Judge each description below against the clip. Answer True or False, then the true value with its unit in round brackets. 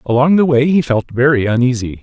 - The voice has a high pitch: False (130 Hz)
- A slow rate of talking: False (205 wpm)